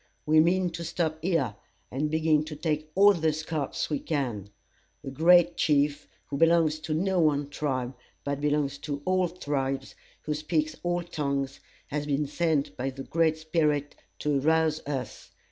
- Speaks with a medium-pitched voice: Yes, medium, 155 Hz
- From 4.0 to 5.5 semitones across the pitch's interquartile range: No, narrow, 2.5 semitones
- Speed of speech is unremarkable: Yes, average, 160 wpm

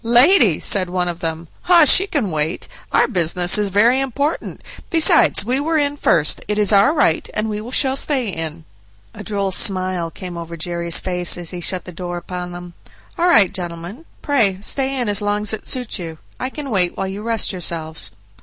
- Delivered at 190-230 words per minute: Yes, average, 200 wpm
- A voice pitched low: No, high, 195 Hz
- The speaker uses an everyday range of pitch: No, wide, 6.2 semitones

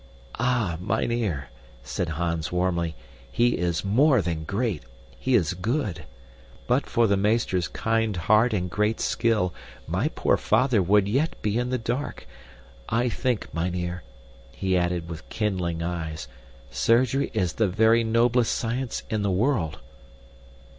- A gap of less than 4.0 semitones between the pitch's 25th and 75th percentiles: No, average, 5.1 semitones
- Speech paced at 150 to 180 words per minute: No, average, 140 wpm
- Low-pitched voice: Yes, low, 105 Hz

